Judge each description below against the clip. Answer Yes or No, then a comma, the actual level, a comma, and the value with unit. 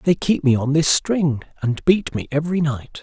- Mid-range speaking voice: Yes, medium, 150 Hz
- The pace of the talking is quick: Yes, fast, 220 wpm